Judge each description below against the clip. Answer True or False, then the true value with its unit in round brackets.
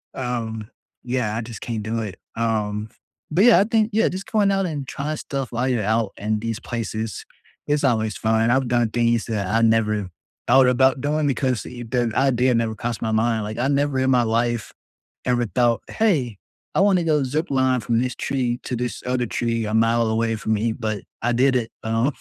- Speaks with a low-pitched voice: True (120 Hz)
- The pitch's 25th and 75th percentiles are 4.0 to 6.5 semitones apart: False (3.0 semitones)